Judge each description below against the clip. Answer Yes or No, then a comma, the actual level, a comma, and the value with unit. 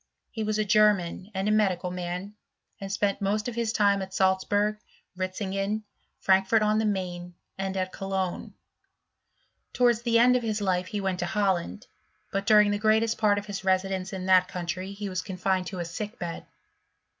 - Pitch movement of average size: No, narrow, 2.2 semitones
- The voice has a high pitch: Yes, high, 195 Hz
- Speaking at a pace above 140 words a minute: Yes, average, 170 wpm